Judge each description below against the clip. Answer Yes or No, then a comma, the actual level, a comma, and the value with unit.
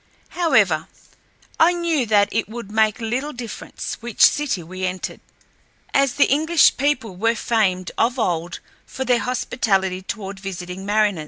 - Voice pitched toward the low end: No, high, 220 Hz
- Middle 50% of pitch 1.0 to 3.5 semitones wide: No, average, 5.0 semitones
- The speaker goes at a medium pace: Yes, average, 145 wpm